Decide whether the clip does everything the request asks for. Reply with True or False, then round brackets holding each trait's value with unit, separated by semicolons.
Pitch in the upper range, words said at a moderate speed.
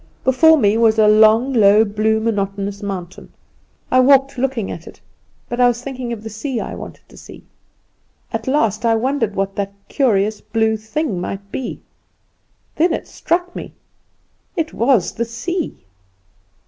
True (225 Hz; 160 wpm)